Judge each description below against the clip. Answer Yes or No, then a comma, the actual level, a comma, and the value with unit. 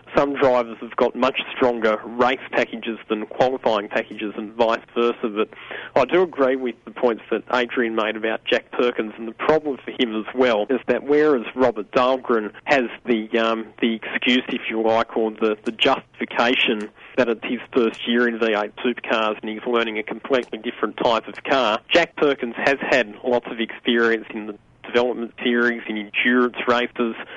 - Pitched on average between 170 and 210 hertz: No, low, 120 Hz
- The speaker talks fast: No, average, 180 wpm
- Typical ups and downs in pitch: No, narrow, 2.1 semitones